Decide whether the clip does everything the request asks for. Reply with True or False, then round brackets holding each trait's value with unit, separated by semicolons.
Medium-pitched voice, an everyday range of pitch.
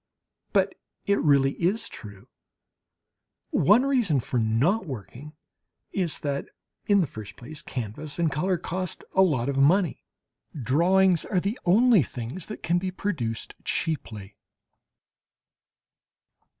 False (155 Hz; 6.9 semitones)